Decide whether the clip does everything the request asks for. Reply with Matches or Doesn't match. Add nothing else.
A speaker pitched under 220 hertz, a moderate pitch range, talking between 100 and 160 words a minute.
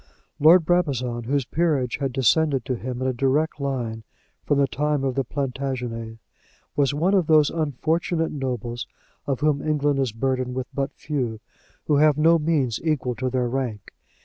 Doesn't match